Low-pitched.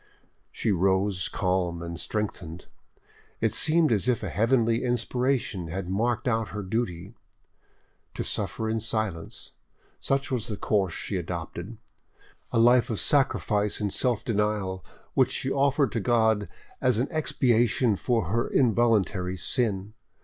Yes: low, 110 Hz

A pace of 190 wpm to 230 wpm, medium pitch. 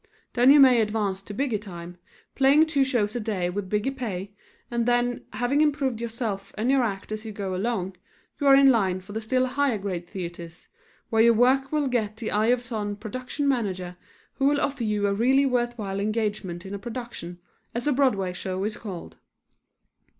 No: average, 195 wpm; high, 220 Hz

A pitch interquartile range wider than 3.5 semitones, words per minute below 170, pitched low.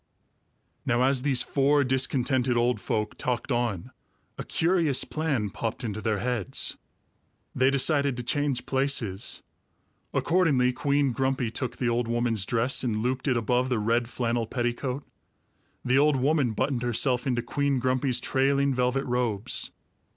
No: narrow, 2.5 semitones; average, 145 wpm; low, 125 Hz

